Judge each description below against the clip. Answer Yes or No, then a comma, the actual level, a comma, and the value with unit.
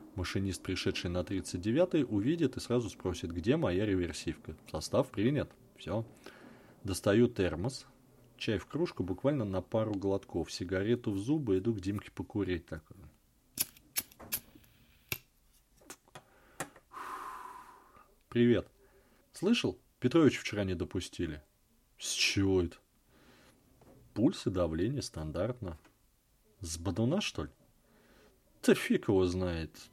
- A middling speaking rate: No, slow, 105 wpm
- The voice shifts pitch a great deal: No, average, 4.7 semitones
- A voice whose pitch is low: Yes, low, 100 Hz